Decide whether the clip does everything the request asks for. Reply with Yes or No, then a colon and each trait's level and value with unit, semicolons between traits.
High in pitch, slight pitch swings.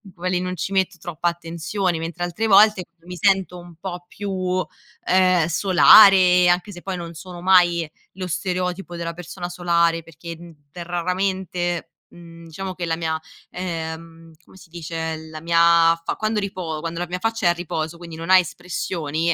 No: medium, 175 Hz; narrow, 1.7 semitones